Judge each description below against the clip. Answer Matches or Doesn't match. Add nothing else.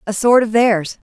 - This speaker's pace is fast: Matches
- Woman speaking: Matches